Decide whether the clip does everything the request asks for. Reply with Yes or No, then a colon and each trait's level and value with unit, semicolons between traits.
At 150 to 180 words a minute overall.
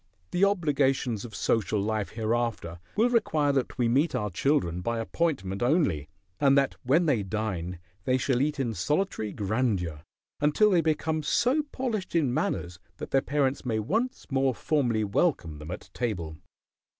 Yes: average, 160 wpm